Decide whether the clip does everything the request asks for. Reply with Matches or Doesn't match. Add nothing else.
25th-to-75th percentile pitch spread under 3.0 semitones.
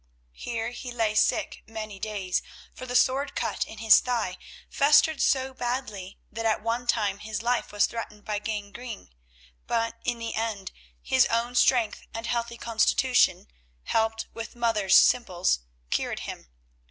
Matches